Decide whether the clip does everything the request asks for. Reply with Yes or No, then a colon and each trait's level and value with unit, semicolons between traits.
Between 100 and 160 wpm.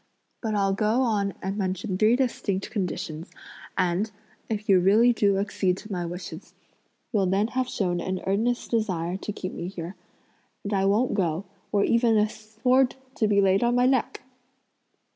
No: average, 170 wpm